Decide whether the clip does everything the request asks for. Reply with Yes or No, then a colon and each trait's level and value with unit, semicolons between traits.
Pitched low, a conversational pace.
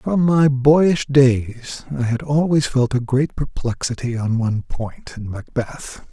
Yes: low, 130 Hz; average, 155 wpm